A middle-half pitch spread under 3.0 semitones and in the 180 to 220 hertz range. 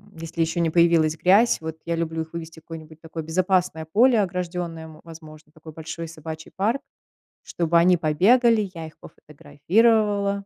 No: narrow, 2.6 semitones; medium, 165 Hz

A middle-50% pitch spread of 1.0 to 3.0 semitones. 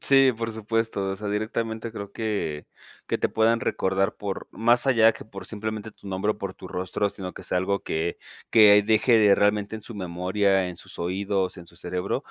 Yes: average, 2.7 semitones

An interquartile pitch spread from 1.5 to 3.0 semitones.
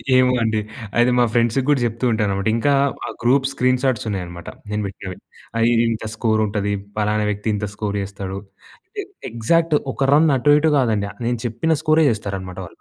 No: average, 3.9 semitones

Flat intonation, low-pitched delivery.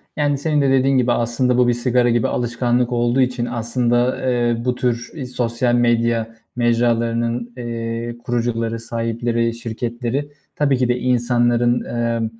Yes: narrow, 1.0 semitones; low, 120 Hz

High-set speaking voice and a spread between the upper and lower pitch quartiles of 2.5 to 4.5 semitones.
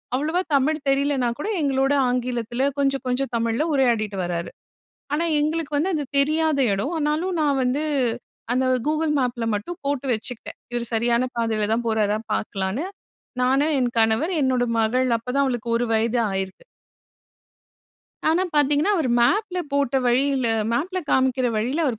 Yes: very high, 260 Hz; average, 3.9 semitones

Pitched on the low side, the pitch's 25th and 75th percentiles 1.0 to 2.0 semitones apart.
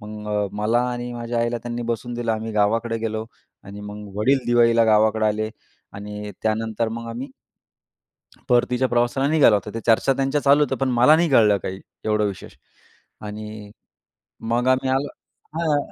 No: low, 115 Hz; narrow, 2.4 semitones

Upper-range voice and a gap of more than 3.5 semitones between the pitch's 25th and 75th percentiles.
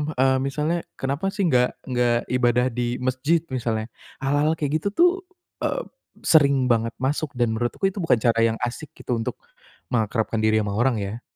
No: low, 125 Hz; average, 4.0 semitones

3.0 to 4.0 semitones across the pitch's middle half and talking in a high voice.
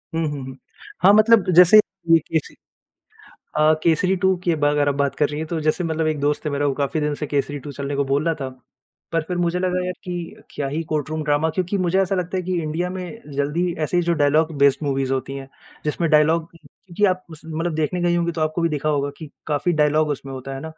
No: average, 3.3 semitones; medium, 155 Hz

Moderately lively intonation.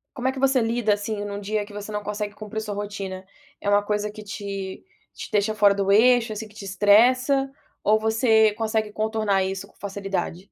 No: narrow, 1.5 semitones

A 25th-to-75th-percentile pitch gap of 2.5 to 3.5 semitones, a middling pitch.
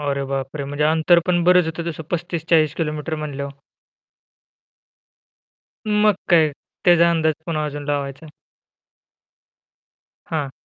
Yes: average, 2.8 semitones; medium, 155 Hz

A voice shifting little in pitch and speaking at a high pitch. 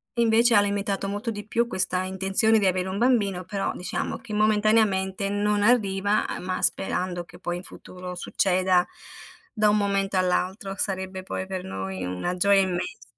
Yes: narrow, 2.1 semitones; high, 195 Hz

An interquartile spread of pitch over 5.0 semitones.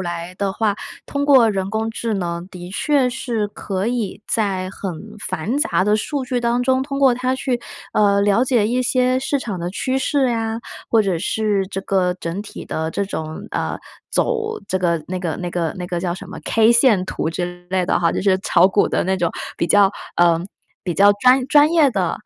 Yes: wide, 5.4 semitones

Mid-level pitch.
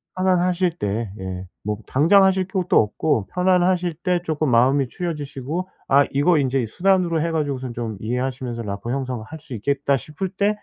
Yes: medium, 145 Hz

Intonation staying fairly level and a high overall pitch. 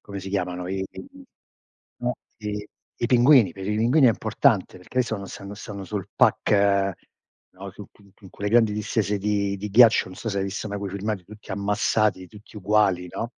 No: narrow, 2.0 semitones; low, 105 Hz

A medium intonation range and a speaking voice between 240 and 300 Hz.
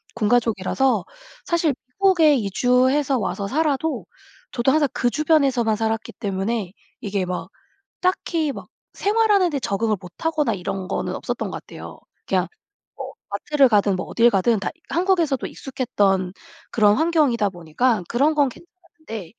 No: wide, 7.0 semitones; high, 245 Hz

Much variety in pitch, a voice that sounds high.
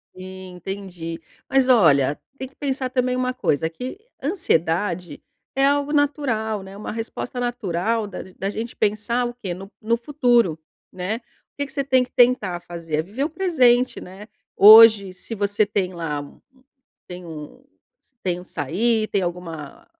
Yes: wide, 5.9 semitones; high, 210 Hz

